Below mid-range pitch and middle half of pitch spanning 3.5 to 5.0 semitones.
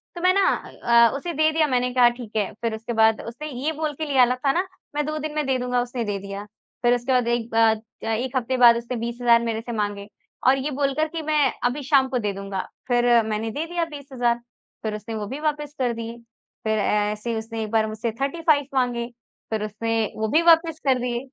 No: high, 245 Hz; average, 4.2 semitones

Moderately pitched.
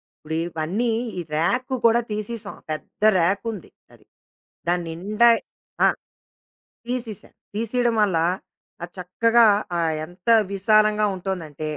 No: high, 205 Hz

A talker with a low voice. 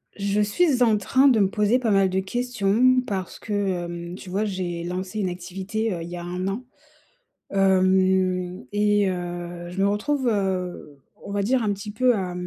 No: high, 195 Hz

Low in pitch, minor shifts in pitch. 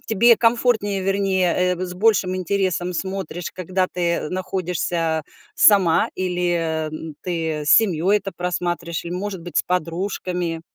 No: medium, 180 Hz; narrow, 2.2 semitones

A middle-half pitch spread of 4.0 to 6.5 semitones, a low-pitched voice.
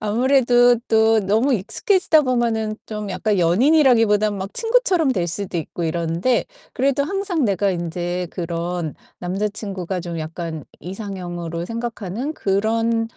No: wide, 5.5 semitones; high, 210 Hz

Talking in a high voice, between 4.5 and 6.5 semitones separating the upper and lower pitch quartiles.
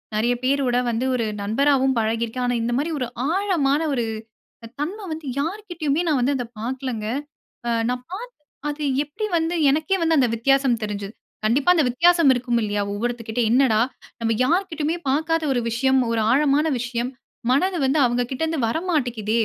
Yes: very high, 265 Hz; average, 4.9 semitones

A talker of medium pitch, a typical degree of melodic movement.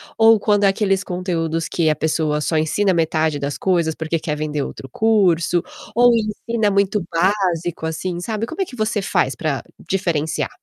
Yes: medium, 175 Hz; average, 4.5 semitones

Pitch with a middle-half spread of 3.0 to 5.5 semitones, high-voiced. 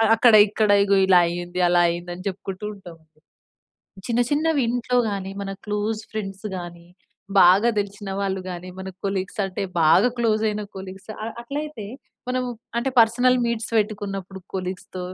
Yes: average, 3.3 semitones; high, 200 Hz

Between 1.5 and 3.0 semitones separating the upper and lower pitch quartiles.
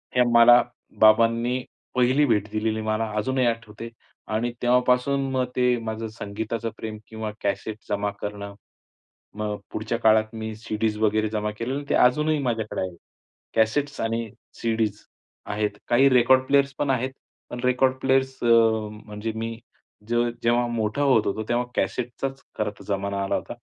Yes: narrow, 2.6 semitones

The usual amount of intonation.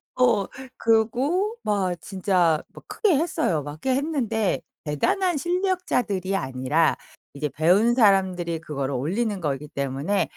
No: wide, 8.3 semitones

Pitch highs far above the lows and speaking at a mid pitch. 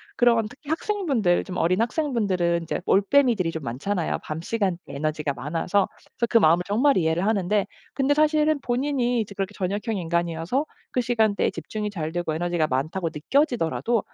No: wide, 6.3 semitones; high, 200 Hz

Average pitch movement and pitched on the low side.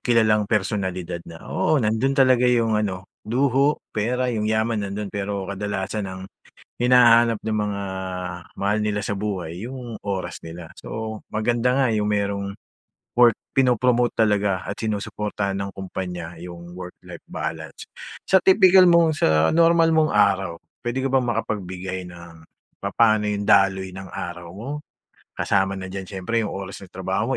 Yes: average, 4.0 semitones; low, 105 Hz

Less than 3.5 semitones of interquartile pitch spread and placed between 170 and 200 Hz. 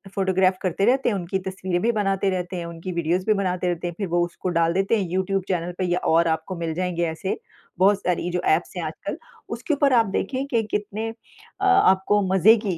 Yes: average, 2.9 semitones; high, 190 Hz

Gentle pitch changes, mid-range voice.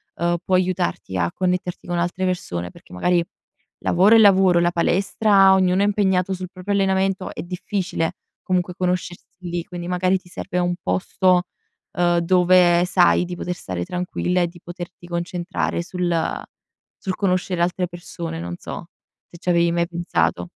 Yes: narrow, 1.2 semitones; medium, 180 Hz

